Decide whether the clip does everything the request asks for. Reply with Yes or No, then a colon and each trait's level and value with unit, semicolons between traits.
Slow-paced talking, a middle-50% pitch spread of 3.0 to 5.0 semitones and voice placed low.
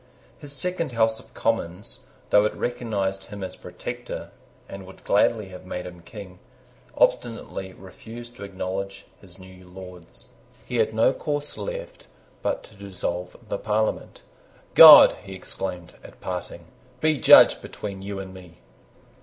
No: average, 145 wpm; average, 3.5 semitones; low, 100 Hz